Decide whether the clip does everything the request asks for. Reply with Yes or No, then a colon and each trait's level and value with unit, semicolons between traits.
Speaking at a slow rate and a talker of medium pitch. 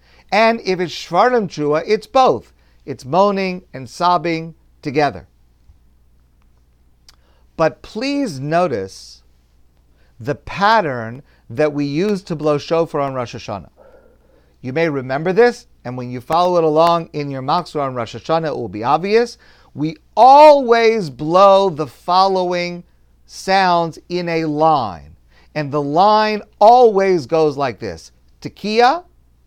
Yes: slow, 125 wpm; medium, 150 Hz